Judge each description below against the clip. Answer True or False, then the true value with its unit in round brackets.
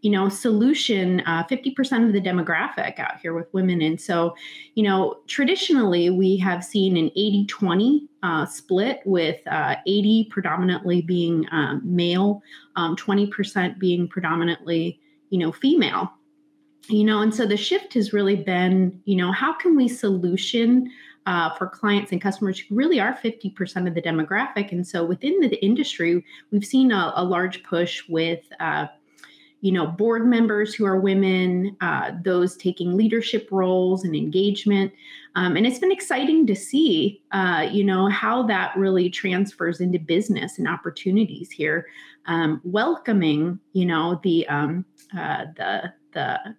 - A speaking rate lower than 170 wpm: True (155 wpm)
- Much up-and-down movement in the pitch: False (3.7 semitones)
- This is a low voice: False (195 Hz)